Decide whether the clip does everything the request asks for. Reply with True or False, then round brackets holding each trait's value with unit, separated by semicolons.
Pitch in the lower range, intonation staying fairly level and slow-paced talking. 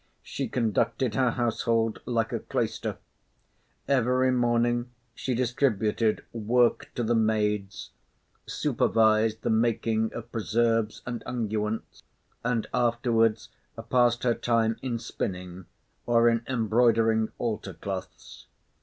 True (115 Hz; 1.6 semitones; 110 wpm)